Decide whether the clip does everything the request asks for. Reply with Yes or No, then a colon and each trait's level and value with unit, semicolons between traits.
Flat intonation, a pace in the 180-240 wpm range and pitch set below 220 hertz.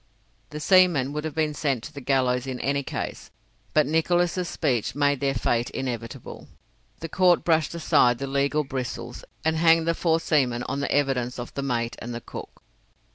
No: average, 4.1 semitones; average, 185 wpm; medium, 140 Hz